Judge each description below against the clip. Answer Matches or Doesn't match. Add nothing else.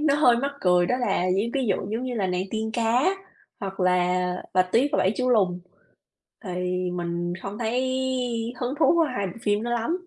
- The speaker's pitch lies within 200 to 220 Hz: Matches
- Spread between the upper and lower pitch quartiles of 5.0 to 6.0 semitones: Matches